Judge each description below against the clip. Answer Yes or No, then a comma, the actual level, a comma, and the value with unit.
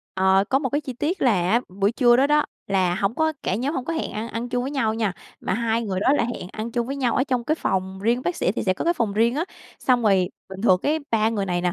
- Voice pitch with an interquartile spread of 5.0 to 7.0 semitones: Yes, average, 5.3 semitones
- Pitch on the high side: Yes, high, 230 Hz